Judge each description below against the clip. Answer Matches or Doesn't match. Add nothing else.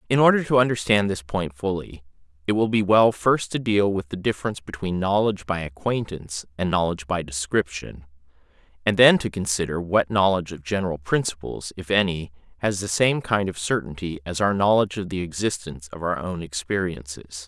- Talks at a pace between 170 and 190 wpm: Matches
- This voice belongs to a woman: Doesn't match